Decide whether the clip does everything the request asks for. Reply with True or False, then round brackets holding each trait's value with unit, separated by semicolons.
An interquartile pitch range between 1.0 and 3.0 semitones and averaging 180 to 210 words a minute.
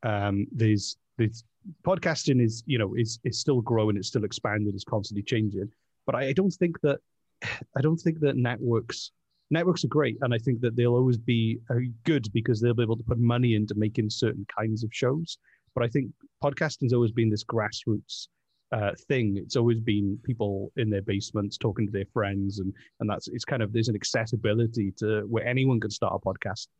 False (3.5 semitones; 200 wpm)